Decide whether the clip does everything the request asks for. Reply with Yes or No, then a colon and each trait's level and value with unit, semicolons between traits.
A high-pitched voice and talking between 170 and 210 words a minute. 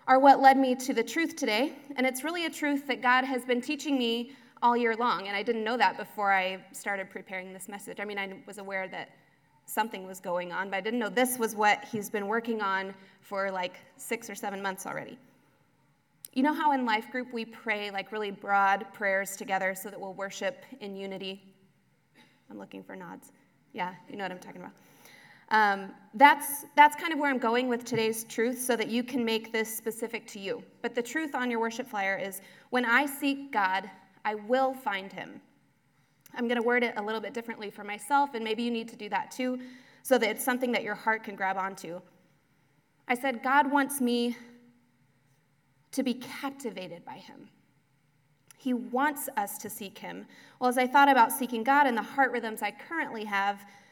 Yes: high, 220 Hz; fast, 205 wpm